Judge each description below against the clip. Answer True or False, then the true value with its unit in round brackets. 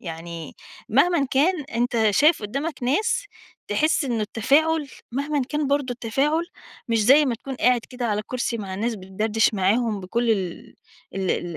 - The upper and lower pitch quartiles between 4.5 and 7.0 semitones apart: True (5.3 semitones)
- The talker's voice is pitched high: True (240 Hz)